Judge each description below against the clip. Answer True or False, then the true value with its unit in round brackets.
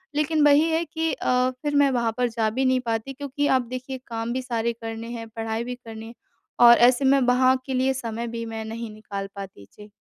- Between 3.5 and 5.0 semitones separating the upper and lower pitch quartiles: False (2.8 semitones)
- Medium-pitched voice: False (235 Hz)